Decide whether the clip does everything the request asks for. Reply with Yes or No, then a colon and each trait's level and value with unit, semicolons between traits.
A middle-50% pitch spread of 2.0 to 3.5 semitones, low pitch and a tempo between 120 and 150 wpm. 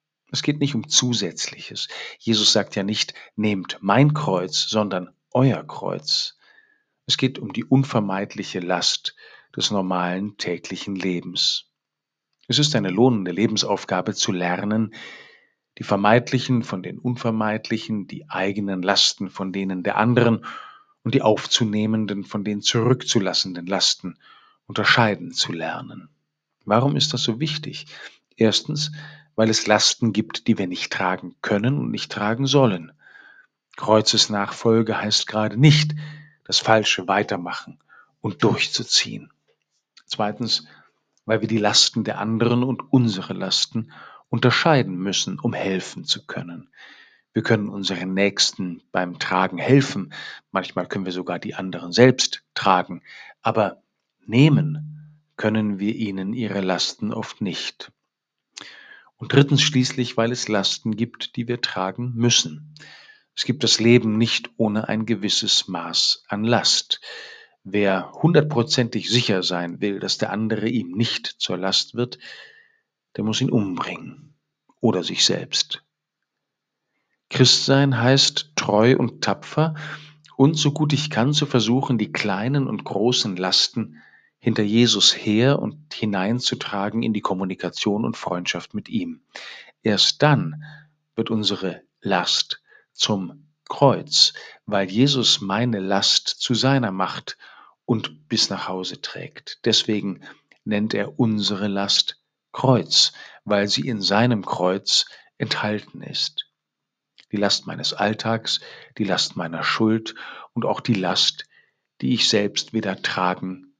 No: average, 4.6 semitones; low, 110 Hz; average, 130 wpm